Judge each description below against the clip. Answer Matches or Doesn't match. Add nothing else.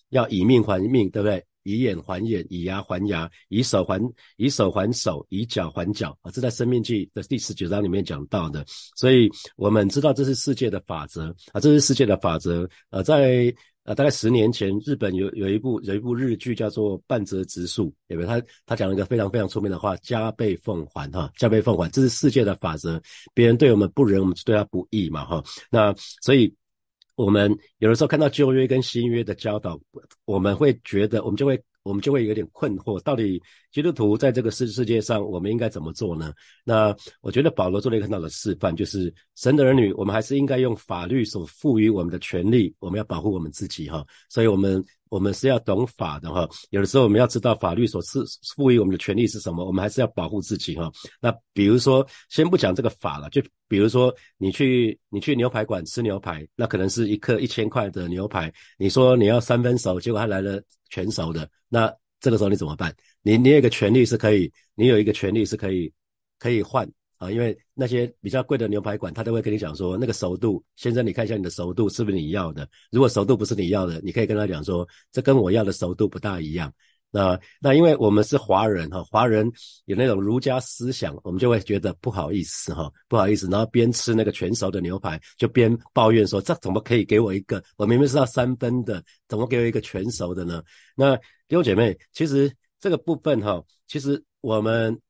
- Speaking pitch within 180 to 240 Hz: Doesn't match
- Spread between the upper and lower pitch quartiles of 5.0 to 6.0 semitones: Doesn't match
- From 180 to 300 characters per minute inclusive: Doesn't match